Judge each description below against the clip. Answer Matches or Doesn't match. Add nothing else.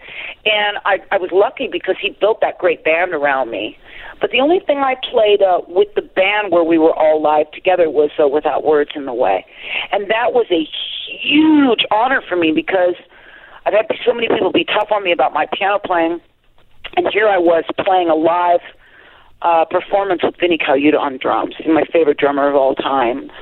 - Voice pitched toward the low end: Doesn't match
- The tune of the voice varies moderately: Doesn't match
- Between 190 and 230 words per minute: Matches